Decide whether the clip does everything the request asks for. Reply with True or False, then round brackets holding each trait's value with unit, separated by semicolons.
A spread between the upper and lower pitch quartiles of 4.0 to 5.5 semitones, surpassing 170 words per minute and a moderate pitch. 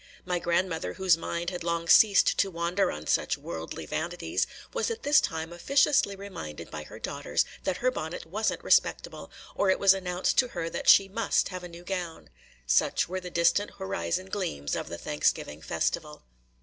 False (2.8 semitones; 185 wpm; 180 Hz)